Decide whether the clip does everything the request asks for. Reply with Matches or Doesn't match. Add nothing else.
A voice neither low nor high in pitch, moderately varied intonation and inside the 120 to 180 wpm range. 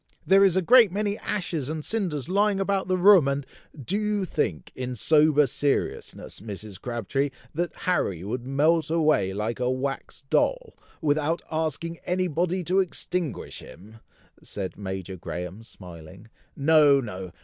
Doesn't match